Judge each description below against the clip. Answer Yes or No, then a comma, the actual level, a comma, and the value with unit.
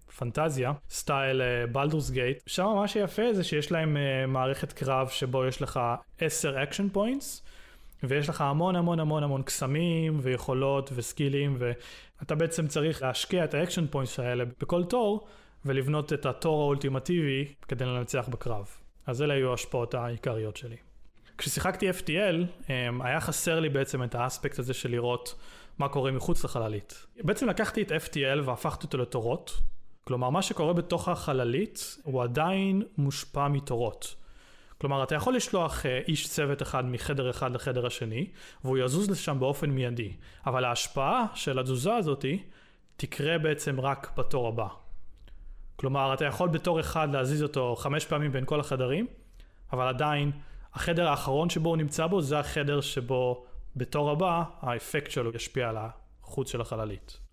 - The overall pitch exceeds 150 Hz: No, medium, 140 Hz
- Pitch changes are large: No, average, 4.3 semitones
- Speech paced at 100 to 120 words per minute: No, average, 145 wpm